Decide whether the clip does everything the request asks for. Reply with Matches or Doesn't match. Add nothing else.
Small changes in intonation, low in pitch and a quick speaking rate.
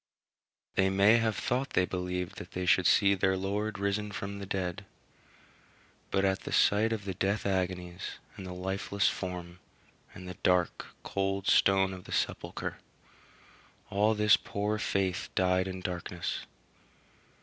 Doesn't match